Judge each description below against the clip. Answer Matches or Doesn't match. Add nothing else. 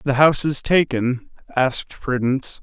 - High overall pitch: Doesn't match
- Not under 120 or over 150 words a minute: Matches